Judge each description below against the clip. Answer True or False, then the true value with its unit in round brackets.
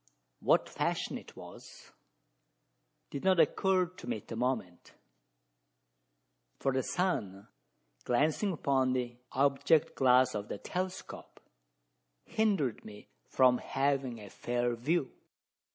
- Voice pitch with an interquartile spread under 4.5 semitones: False (5.2 semitones)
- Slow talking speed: True (115 wpm)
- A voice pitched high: False (135 Hz)